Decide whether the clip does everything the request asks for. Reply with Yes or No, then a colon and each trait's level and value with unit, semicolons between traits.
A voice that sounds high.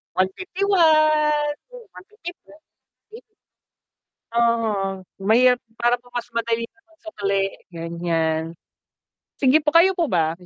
Yes: high, 235 Hz